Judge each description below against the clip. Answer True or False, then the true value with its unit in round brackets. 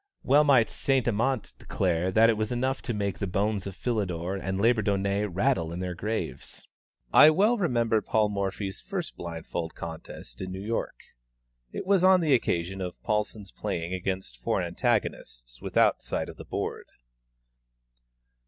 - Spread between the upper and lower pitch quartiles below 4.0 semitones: False (4.7 semitones)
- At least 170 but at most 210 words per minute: False (155 wpm)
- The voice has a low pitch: True (100 Hz)